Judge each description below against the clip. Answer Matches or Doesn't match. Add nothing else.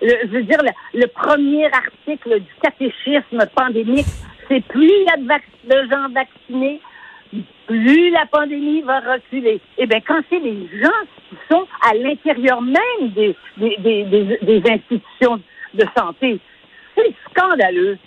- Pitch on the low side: Doesn't match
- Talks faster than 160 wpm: Doesn't match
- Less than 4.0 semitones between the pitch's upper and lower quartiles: Doesn't match